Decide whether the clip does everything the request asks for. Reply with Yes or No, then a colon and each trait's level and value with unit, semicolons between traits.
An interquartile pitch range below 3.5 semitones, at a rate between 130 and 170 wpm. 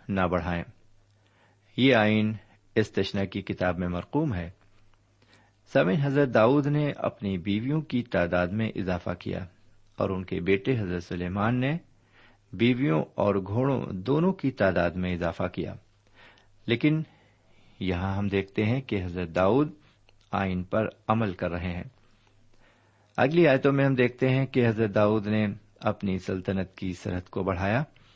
No: average, 4.0 semitones; average, 145 wpm